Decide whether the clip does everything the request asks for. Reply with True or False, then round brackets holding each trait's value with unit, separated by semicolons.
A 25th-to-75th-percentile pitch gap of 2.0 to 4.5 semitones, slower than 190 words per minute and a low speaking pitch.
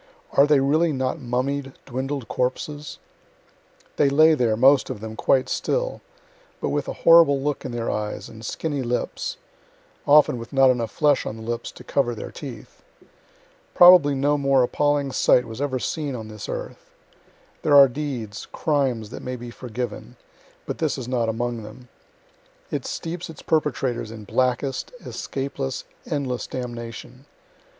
True (3.3 semitones; 155 wpm; 130 Hz)